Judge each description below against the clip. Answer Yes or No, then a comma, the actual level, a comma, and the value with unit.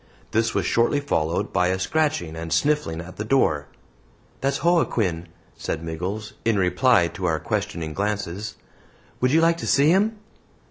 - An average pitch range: No, wide, 8.6 semitones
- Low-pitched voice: Yes, low, 105 Hz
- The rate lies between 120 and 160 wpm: Yes, average, 155 wpm